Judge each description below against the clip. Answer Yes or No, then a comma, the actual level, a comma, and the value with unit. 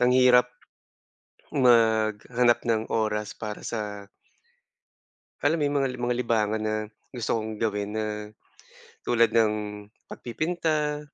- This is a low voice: Yes, low, 115 Hz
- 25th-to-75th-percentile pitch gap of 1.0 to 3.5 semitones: Yes, narrow, 2.6 semitones